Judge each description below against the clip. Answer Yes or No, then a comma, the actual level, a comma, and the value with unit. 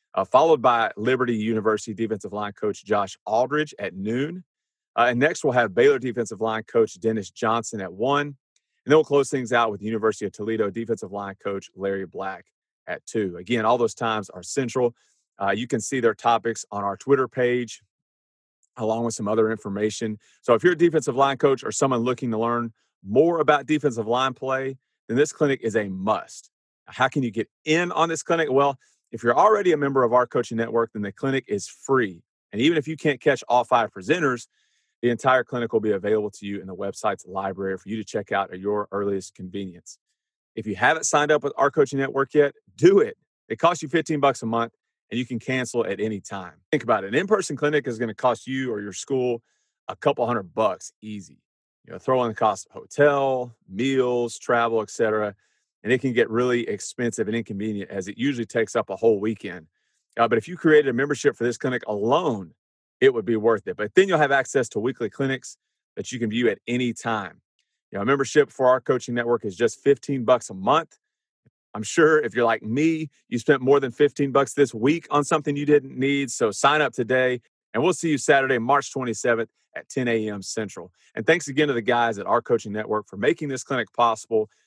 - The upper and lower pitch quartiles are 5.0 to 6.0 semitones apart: No, average, 4.2 semitones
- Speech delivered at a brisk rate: Yes, fast, 215 wpm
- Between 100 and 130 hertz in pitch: Yes, low, 120 Hz